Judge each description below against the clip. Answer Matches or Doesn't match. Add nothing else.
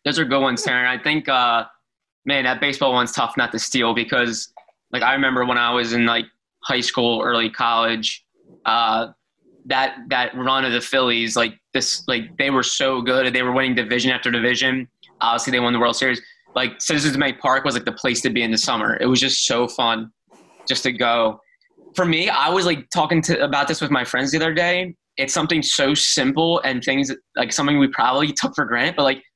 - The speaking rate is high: Matches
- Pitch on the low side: Matches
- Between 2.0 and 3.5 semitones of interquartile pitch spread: Matches